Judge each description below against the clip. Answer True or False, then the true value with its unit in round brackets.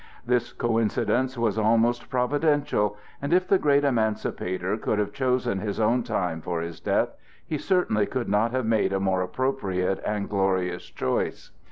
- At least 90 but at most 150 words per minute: False (160 wpm)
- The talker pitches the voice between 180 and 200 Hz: False (110 Hz)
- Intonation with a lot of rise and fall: False (4.6 semitones)